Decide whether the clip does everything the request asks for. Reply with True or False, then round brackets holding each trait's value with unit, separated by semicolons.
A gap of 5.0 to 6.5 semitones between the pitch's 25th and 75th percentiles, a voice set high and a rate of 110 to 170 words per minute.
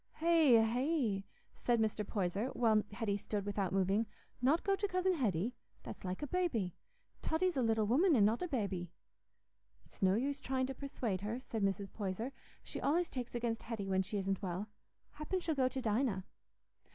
False (5.6 semitones; 225 Hz; 180 wpm)